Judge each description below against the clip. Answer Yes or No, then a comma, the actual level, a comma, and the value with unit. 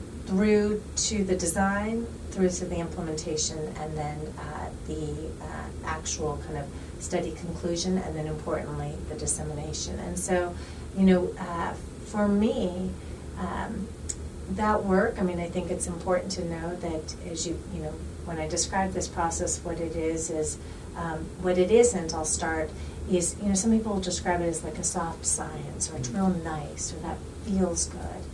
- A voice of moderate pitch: Yes, medium, 170 Hz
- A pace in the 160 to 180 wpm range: Yes, average, 175 wpm